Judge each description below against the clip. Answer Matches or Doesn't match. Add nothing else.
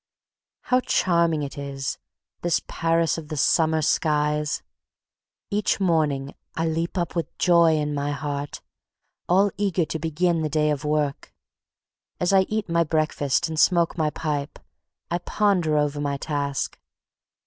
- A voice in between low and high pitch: Matches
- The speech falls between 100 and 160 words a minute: Matches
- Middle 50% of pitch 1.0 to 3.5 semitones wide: Matches